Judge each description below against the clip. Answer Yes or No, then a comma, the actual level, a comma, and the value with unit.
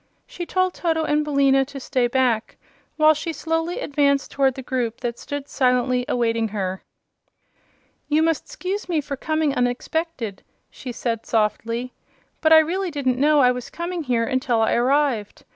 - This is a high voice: Yes, very high, 275 Hz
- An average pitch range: Yes, average, 4.4 semitones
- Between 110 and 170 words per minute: Yes, average, 160 wpm